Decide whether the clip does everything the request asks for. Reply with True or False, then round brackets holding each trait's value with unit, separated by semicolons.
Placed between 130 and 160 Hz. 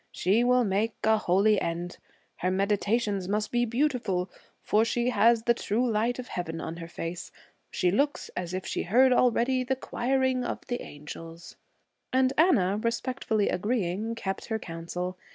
False (215 Hz)